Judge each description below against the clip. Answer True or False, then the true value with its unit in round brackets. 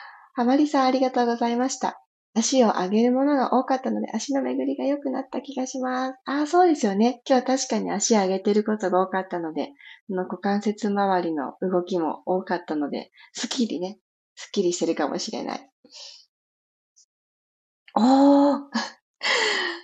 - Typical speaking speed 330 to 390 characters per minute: True (335 characters per minute)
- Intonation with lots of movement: True (5.9 semitones)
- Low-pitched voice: False (245 Hz)